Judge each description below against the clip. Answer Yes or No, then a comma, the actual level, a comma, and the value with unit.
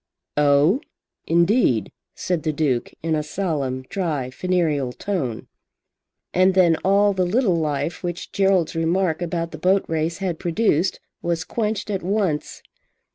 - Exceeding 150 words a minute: No, slow, 135 wpm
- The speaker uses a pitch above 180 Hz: No, medium, 170 Hz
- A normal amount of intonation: Yes, average, 3.9 semitones